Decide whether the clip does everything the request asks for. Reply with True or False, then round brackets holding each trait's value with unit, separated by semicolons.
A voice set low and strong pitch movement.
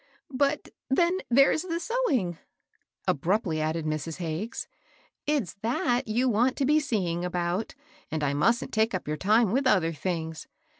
False (215 Hz; 7.8 semitones)